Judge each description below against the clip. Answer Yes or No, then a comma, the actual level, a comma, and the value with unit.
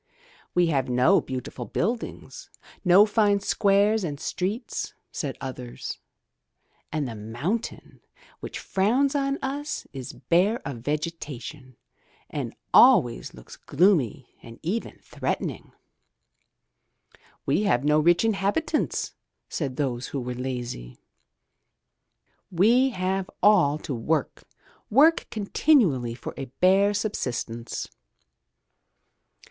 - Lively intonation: Yes, wide, 8.2 semitones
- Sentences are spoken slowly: Yes, slow, 105 wpm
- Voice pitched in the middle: Yes, medium, 170 Hz